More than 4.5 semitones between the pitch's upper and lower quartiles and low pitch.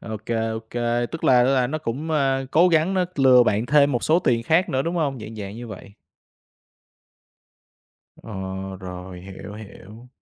Yes: average, 5.0 semitones; low, 125 Hz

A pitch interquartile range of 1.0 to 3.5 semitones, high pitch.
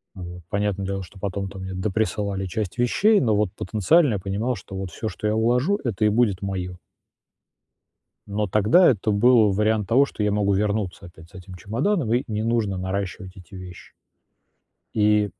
No: average, 2.7 semitones; low, 105 Hz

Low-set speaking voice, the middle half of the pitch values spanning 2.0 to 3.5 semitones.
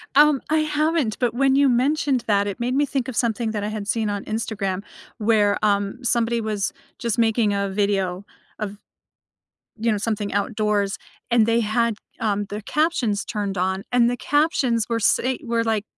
No: high, 225 Hz; average, 3.2 semitones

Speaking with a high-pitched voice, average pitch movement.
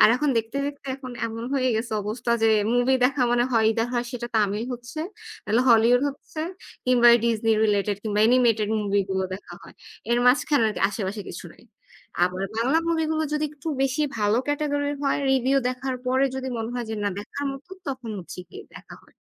Yes: high, 240 Hz; average, 3.5 semitones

